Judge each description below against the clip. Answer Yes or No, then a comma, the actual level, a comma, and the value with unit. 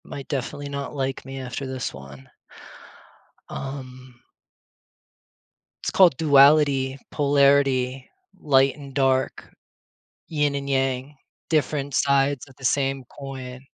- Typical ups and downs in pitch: No, narrow, 1.4 semitones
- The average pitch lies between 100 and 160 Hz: Yes, low, 135 Hz